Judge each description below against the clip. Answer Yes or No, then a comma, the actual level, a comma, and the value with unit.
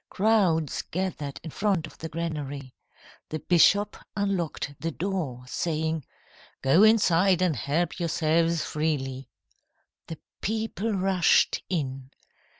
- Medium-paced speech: No, slow, 110 wpm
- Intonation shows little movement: No, average, 4.1 semitones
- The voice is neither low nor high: Yes, medium, 165 Hz